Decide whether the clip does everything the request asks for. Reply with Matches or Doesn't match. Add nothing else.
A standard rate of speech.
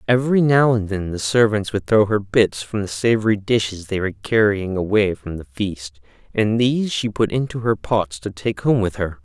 Doesn't match